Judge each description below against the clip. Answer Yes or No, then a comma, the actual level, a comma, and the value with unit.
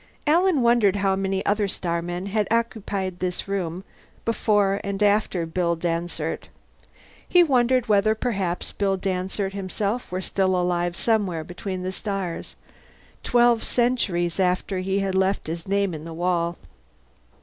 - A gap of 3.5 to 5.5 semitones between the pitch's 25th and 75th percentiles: No, average, 2.9 semitones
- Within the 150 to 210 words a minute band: No, average, 140 wpm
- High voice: Yes, high, 195 Hz